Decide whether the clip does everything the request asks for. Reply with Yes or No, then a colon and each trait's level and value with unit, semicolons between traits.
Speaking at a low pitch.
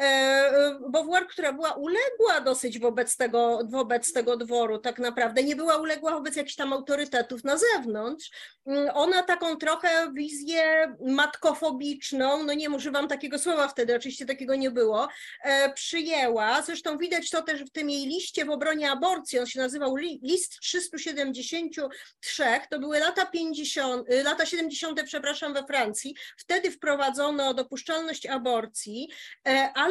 No: very high, 290 Hz